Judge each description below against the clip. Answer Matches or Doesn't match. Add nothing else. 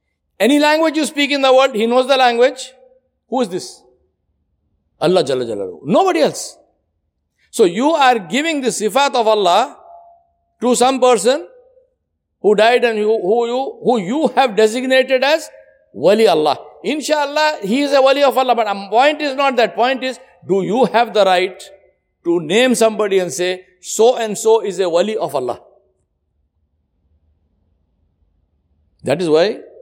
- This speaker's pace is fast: Doesn't match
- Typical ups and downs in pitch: Doesn't match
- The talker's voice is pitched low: Doesn't match